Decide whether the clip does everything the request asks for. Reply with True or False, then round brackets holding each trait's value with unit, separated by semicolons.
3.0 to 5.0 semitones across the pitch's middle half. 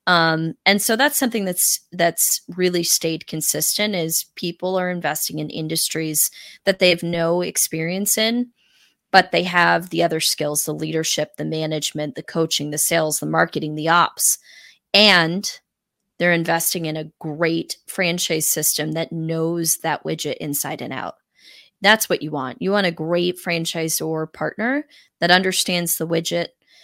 False (2.4 semitones)